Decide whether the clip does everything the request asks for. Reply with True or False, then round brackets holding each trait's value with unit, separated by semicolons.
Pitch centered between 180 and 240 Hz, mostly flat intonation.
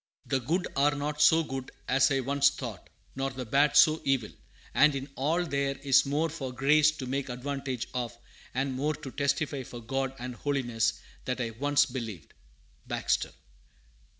False (135 Hz; 2.2 semitones)